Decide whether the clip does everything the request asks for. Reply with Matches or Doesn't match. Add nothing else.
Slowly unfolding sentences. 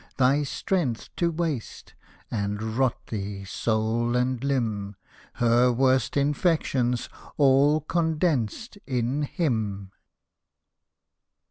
Matches